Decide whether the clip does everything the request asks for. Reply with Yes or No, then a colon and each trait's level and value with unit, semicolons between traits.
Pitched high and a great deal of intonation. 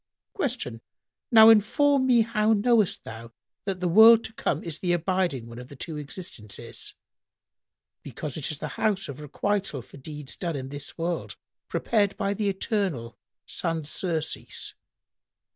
No: medium, 175 Hz; wide, 6.7 semitones